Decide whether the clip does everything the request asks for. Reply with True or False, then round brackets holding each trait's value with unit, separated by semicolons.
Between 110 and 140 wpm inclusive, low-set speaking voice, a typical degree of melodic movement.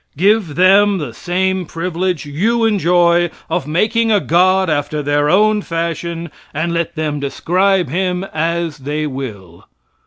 False (135 wpm; 170 Hz; 3.7 semitones)